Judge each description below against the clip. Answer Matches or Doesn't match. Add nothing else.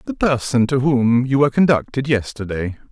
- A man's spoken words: Matches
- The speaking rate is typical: Matches